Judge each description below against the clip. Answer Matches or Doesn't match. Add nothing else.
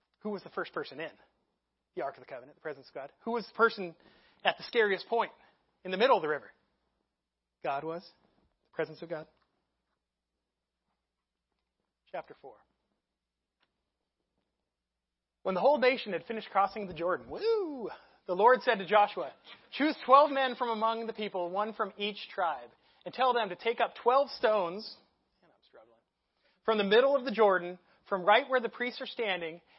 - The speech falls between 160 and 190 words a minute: Matches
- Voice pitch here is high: Matches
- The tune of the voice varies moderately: Doesn't match